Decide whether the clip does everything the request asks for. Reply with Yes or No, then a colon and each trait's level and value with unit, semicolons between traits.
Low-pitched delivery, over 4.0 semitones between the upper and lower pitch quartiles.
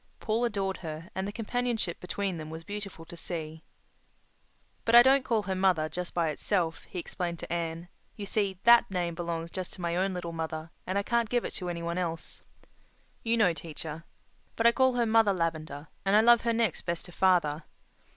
No: medium, 180 Hz; average, 4.4 semitones